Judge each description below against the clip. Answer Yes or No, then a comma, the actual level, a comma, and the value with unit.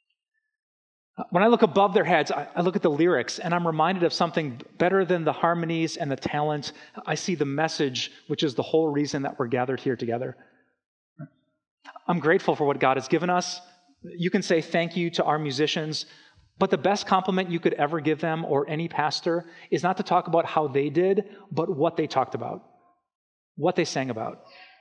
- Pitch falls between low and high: Yes, medium, 165 Hz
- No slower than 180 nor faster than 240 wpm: Yes, average, 200 wpm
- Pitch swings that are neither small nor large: Yes, average, 3.3 semitones